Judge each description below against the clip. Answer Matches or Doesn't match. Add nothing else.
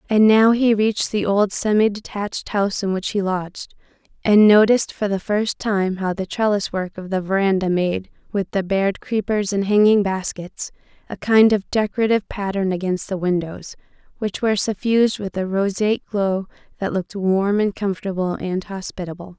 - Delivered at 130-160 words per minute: Doesn't match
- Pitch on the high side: Matches